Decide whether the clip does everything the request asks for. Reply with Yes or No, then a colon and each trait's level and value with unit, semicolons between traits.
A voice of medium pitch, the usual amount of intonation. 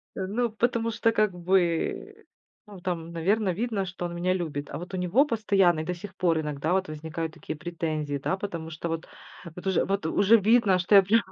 Yes: medium, 180 Hz; average, 3.7 semitones